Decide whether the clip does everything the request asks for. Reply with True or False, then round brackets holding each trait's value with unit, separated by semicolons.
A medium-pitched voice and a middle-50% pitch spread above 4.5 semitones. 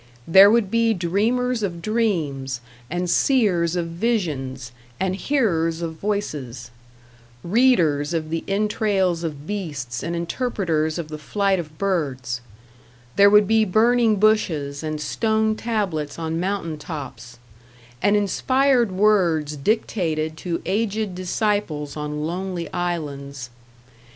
True (175 Hz; 5.5 semitones)